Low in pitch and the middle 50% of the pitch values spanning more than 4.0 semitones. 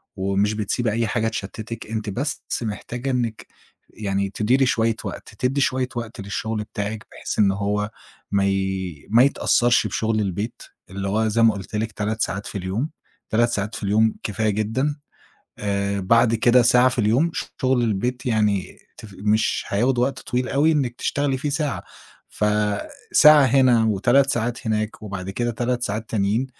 No: low, 110 Hz; average, 3.2 semitones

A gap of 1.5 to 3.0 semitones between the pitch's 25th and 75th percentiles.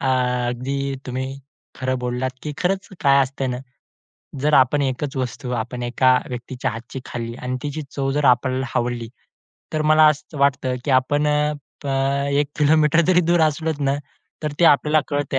Yes: average, 2.7 semitones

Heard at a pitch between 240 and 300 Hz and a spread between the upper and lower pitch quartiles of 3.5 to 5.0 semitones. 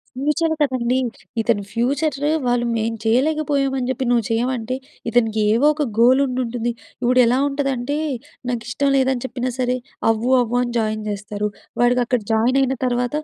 No: high, 245 Hz; narrow, 2.4 semitones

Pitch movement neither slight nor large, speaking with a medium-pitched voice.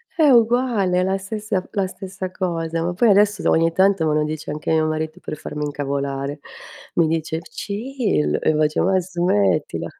Yes: average, 4.2 semitones; medium, 175 Hz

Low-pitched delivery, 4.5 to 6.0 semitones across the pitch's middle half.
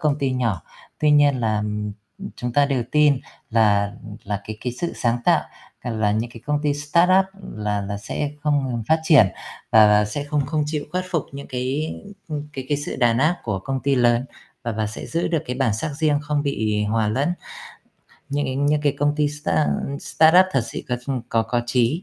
Yes: low, 130 Hz; average, 4.8 semitones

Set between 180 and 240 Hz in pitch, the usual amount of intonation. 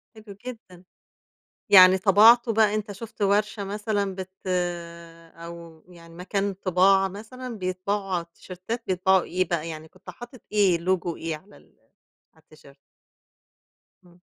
Yes: high, 190 Hz; average, 3.1 semitones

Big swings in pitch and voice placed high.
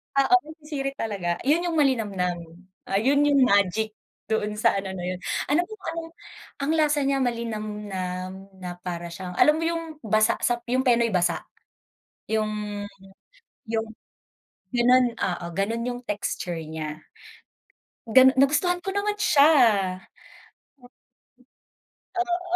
Yes: wide, 6.8 semitones; high, 230 Hz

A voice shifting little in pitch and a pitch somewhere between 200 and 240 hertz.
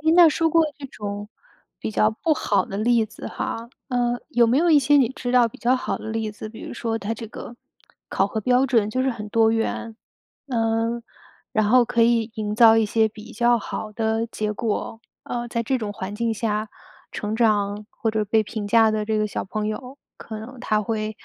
Yes: narrow, 2.0 semitones; high, 225 Hz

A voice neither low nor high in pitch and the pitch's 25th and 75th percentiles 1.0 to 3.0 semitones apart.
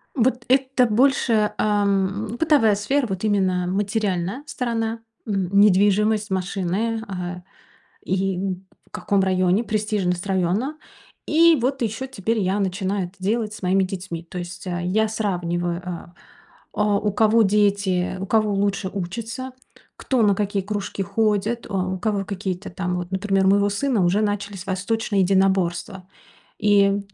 No: high, 200 Hz; average, 2.7 semitones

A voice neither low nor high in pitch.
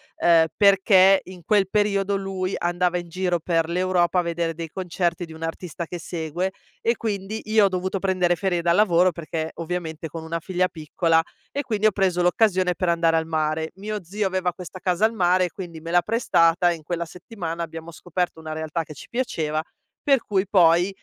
Yes: medium, 175 Hz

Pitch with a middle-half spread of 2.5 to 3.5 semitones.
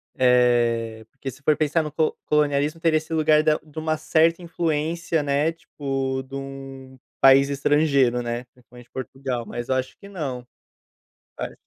Yes: average, 3.2 semitones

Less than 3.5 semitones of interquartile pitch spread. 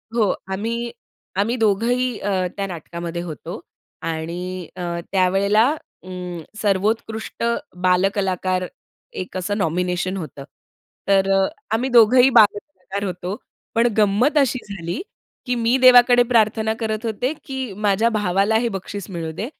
No: average, 3.8 semitones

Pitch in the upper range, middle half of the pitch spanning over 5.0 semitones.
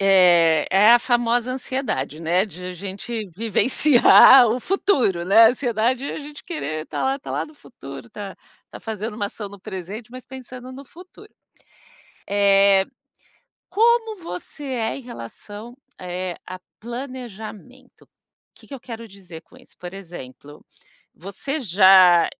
Yes: high, 220 Hz; wide, 5.4 semitones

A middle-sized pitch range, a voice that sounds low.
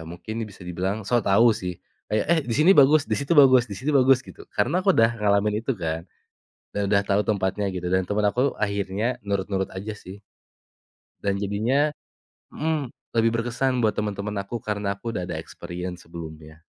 Yes: average, 4.0 semitones; low, 105 Hz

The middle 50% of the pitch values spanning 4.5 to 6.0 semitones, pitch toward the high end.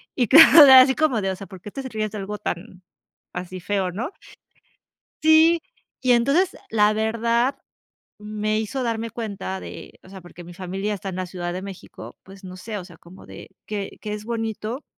No: average, 3.8 semitones; high, 210 Hz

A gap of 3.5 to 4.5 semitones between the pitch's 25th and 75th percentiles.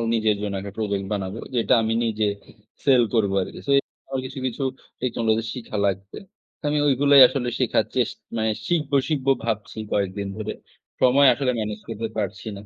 Yes: average, 4.1 semitones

